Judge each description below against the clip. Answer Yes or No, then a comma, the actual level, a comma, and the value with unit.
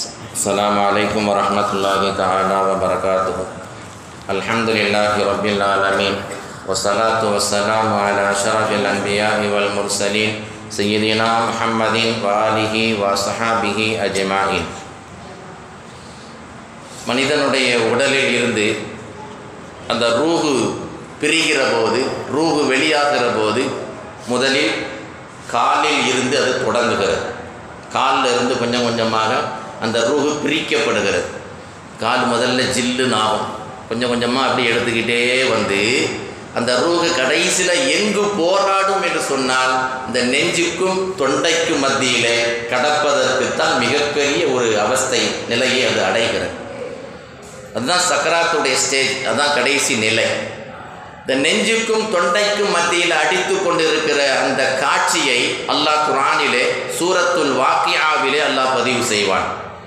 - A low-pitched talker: Yes, low, 115 Hz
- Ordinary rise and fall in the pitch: No, wide, 5.8 semitones